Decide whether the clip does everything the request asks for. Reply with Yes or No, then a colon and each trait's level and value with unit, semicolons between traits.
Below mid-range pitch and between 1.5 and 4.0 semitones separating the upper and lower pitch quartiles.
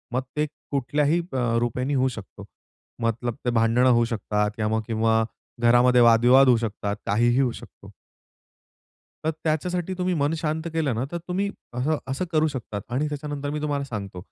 No: low, 130 Hz; average, 4.7 semitones